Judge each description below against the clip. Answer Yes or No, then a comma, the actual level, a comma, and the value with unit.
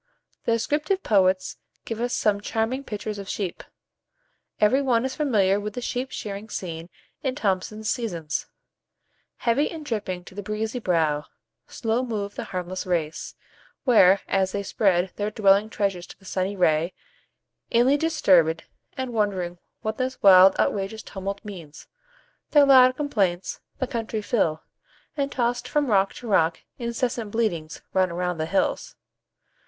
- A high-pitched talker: Yes, high, 205 Hz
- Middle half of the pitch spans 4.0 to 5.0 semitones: Yes, average, 4.5 semitones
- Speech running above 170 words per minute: No, average, 150 wpm